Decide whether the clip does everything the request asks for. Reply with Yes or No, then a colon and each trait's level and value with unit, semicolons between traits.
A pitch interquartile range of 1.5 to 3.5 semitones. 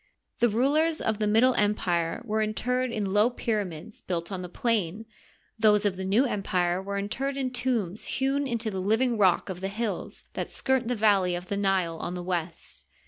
No: average, 4.3 semitones